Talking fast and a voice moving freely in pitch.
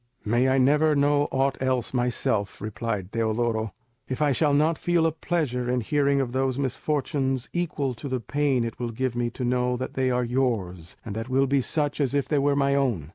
No: fast, 210 wpm; average, 3.1 semitones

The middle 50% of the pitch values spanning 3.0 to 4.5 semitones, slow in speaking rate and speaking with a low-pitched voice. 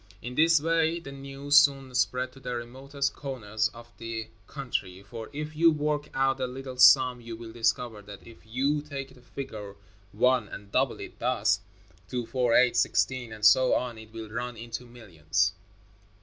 No: average, 3.4 semitones; average, 175 wpm; low, 125 Hz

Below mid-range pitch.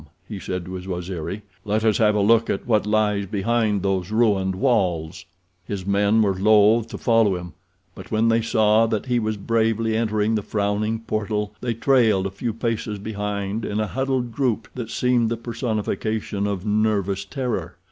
Yes: low, 105 Hz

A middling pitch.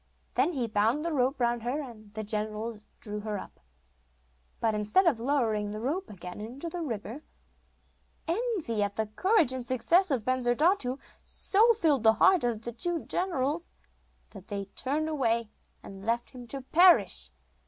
No: high, 245 Hz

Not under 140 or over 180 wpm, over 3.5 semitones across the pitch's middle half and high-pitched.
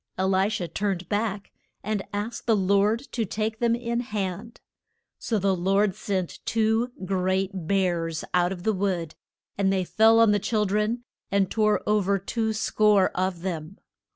No: average, 170 wpm; narrow, 2.6 semitones; high, 200 Hz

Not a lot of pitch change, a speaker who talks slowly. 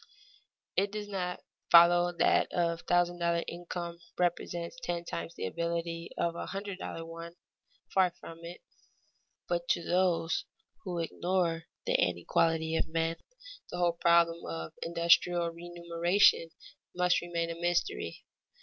Yes: narrow, 0.9 semitones; slow, 130 wpm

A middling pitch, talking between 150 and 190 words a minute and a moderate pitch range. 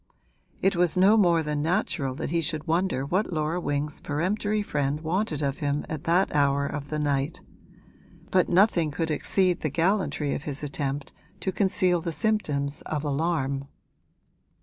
Yes: medium, 155 Hz; average, 160 wpm; average, 3.9 semitones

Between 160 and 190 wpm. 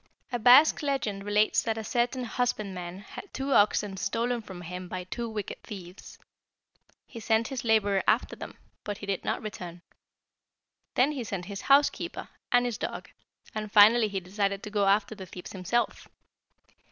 Yes: average, 165 wpm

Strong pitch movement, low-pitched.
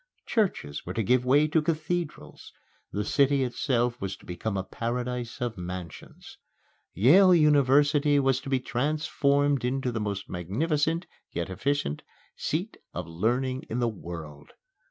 Yes: wide, 6.1 semitones; low, 125 Hz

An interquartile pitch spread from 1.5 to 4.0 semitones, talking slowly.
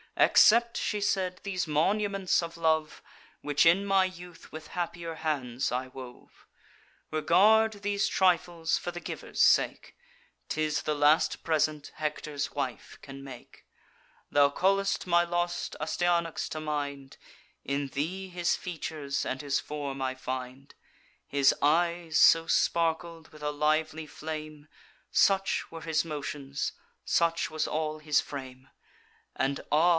Yes: average, 3.2 semitones; slow, 130 wpm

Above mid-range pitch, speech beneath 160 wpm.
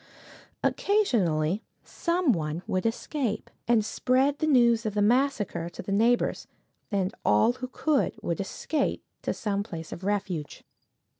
Yes: high, 220 Hz; average, 140 wpm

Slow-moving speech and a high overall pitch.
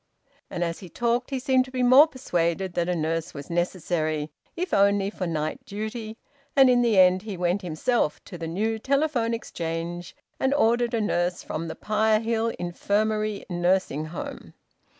No: average, 170 wpm; high, 200 Hz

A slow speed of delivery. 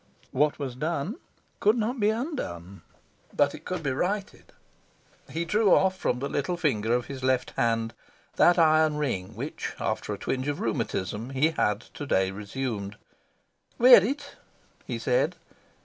No: average, 155 wpm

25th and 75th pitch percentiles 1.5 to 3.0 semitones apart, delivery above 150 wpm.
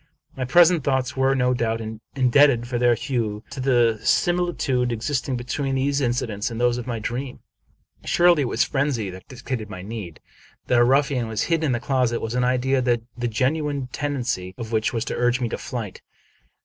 Yes: narrow, 2.6 semitones; average, 190 wpm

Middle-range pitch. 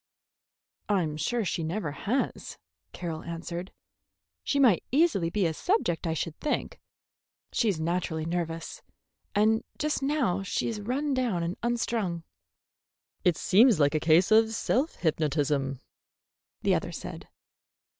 Yes: medium, 180 Hz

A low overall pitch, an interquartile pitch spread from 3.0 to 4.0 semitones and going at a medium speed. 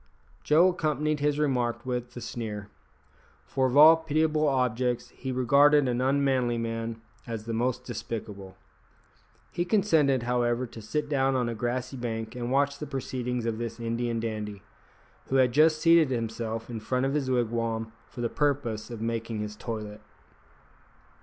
Yes: low, 125 Hz; average, 3.5 semitones; average, 160 wpm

